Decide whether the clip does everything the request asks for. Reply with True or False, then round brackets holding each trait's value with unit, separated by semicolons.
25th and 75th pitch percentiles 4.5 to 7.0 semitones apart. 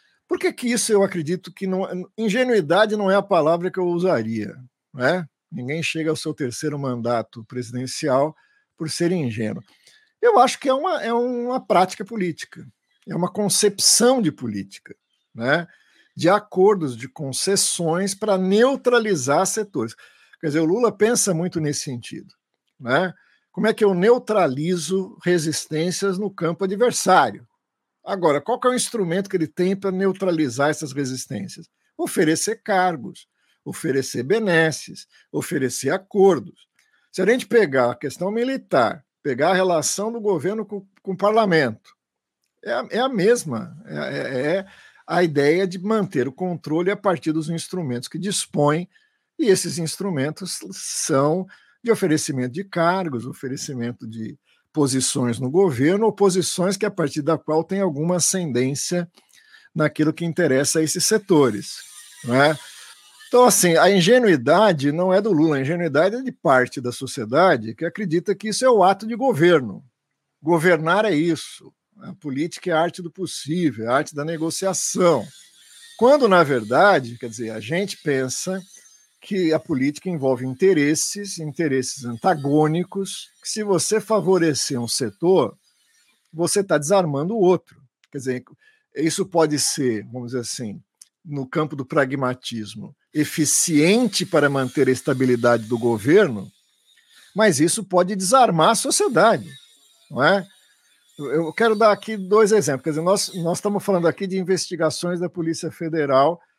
True (5.5 semitones)